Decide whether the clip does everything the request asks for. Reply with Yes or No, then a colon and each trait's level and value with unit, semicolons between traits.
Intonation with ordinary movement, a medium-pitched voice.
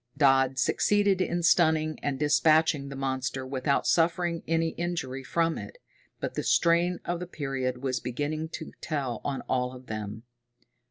Yes: average, 4.1 semitones; medium, 145 Hz